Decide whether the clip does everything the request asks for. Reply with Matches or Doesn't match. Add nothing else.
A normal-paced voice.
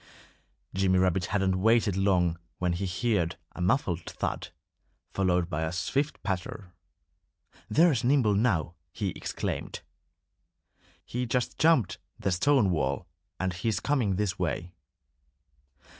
Doesn't match